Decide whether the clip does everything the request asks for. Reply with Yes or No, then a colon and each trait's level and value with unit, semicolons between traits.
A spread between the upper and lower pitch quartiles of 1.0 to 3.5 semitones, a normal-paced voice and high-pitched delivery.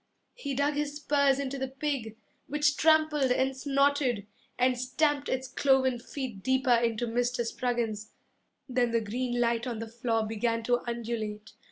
Yes: average, 3.2 semitones; average, 155 wpm; very high, 250 Hz